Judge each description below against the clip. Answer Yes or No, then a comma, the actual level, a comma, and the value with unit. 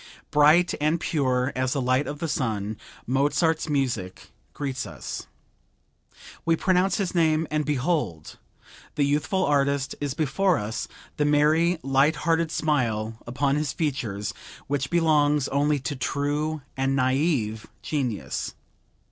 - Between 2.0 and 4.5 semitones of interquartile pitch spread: Yes, average, 3.3 semitones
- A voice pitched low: No, medium, 145 Hz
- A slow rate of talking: Yes, slow, 130 wpm